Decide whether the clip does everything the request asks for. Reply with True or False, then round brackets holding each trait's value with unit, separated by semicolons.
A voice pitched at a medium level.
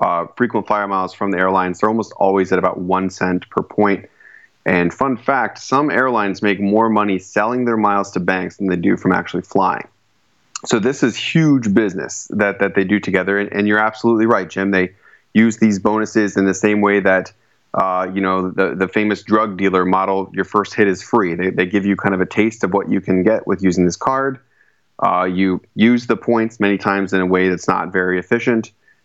False (100 Hz)